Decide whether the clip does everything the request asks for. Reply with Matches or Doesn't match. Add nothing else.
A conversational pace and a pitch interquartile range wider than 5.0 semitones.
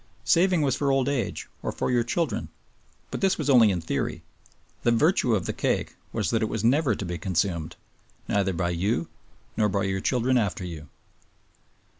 Matches